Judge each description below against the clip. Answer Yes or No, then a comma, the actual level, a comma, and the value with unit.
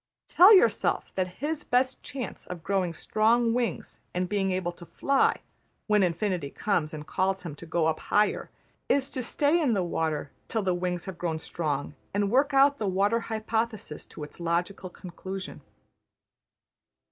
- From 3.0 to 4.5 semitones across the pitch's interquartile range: No, average, 5.0 semitones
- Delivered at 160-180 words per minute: Yes, average, 165 wpm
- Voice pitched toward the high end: Yes, high, 195 Hz